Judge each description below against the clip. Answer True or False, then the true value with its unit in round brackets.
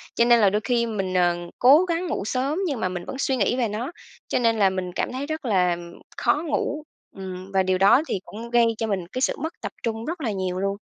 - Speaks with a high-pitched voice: True (225 Hz)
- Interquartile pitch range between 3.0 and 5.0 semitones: False (5.5 semitones)